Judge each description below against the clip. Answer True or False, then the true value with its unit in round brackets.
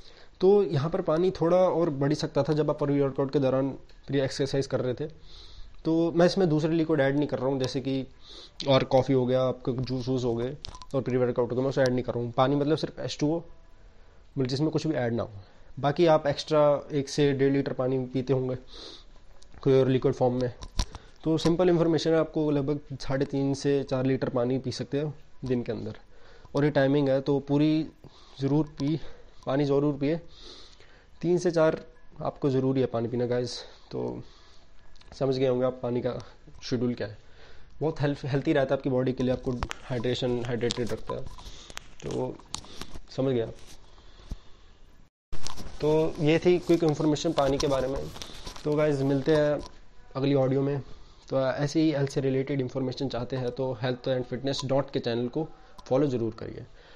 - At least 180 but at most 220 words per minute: True (190 wpm)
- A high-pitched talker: False (135 Hz)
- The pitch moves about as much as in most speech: True (3.2 semitones)